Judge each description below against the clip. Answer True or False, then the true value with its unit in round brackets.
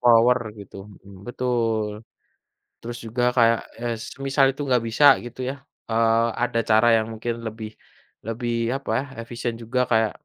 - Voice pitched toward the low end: True (115 Hz)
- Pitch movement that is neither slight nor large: False (1.5 semitones)